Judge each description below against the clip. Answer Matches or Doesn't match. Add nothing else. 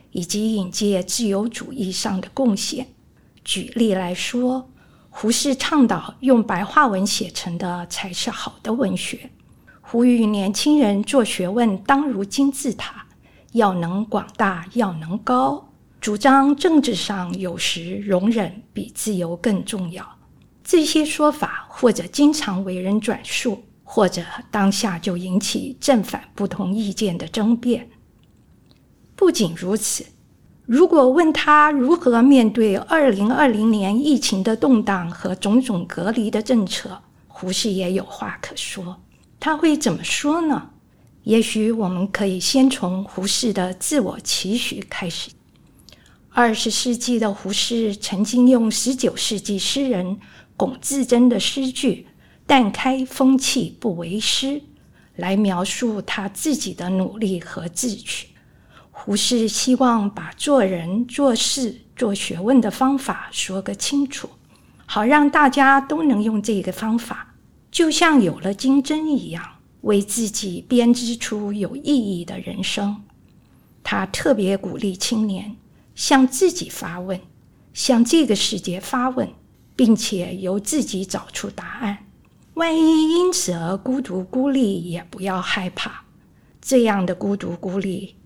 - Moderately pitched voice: Doesn't match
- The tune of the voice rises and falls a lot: Doesn't match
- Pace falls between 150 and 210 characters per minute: Matches